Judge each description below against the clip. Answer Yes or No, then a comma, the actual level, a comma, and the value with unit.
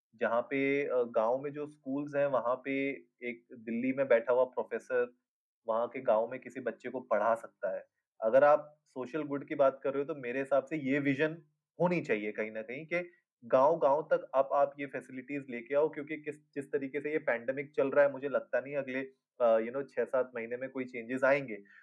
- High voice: No, medium, 140 Hz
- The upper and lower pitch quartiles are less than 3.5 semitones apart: Yes, narrow, 2.5 semitones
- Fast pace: Yes, fast, 215 wpm